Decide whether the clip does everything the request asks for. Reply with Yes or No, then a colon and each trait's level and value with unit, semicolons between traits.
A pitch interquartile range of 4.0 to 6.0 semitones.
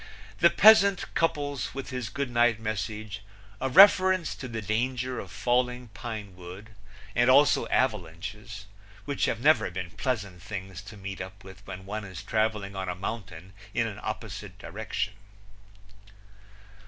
Yes: average, 4.6 semitones